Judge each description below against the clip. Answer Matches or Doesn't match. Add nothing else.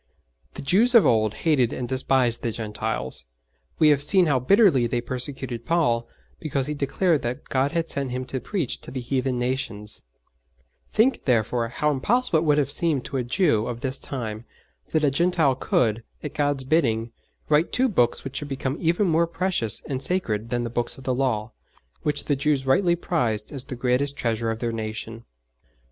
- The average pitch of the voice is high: Doesn't match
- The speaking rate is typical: Matches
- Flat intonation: Doesn't match